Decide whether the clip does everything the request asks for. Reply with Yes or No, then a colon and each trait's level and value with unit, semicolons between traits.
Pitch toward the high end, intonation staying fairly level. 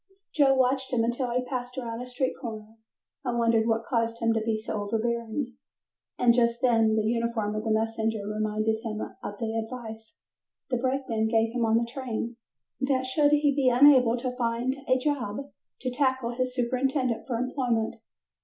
Yes: high, 235 Hz; narrow, 2.3 semitones